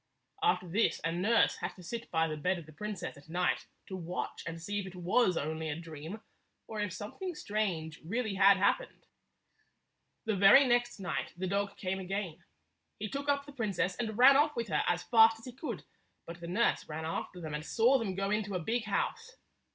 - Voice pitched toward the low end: No, high, 195 Hz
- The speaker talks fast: Yes, fast, 215 wpm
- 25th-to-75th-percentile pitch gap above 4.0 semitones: Yes, average, 5.1 semitones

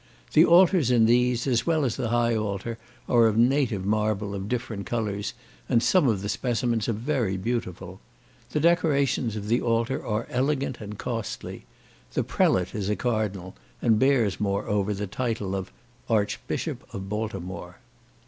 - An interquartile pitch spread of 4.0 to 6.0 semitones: No, average, 3.3 semitones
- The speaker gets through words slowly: No, average, 160 wpm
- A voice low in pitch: Yes, low, 115 Hz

